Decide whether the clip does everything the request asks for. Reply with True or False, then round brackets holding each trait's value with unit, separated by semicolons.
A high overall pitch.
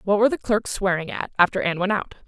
True (195 Hz)